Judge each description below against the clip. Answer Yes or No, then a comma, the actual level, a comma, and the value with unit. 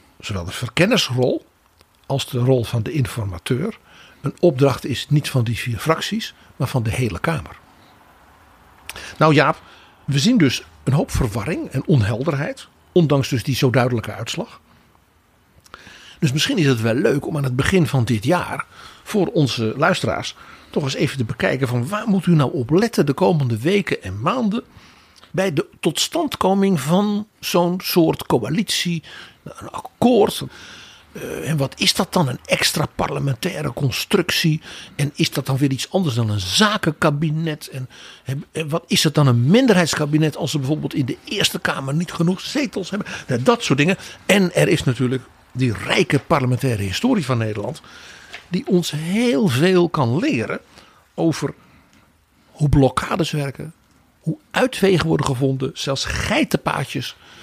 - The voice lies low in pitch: No, medium, 145 Hz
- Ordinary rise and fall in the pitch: No, wide, 5.7 semitones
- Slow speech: No, average, 155 wpm